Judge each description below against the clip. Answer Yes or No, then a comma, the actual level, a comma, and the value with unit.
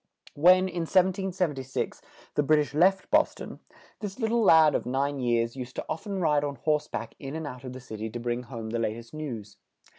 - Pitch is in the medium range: Yes, medium, 145 Hz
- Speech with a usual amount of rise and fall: No, wide, 6.1 semitones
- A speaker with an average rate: No, fast, 220 wpm